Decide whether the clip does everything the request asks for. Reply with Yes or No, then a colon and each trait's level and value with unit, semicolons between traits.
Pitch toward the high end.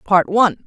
Yes: high, 195 Hz